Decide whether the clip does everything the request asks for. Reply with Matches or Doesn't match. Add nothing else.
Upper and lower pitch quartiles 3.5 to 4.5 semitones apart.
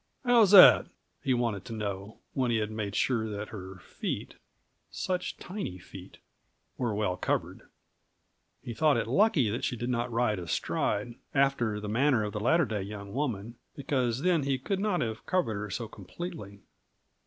Doesn't match